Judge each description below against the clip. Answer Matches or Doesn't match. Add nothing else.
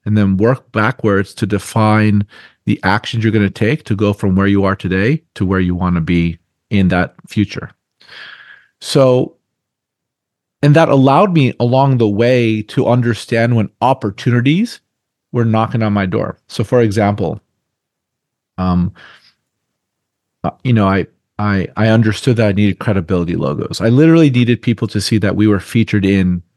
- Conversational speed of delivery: Matches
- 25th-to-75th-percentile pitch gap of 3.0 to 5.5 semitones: Matches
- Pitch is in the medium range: Doesn't match